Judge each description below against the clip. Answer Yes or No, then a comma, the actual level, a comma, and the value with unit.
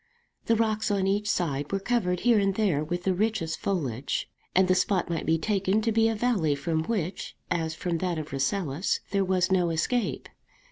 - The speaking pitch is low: No, medium, 185 Hz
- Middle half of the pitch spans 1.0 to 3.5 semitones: No, average, 4.3 semitones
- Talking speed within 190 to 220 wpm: Yes, average, 195 wpm